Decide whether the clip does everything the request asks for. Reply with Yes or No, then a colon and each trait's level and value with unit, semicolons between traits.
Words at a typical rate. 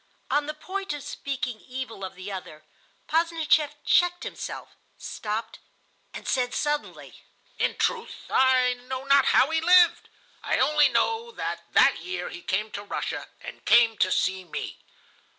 Yes: average, 150 wpm